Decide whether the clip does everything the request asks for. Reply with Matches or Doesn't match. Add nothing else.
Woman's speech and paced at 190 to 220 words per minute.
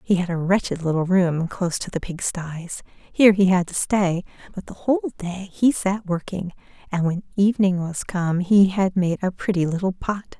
Matches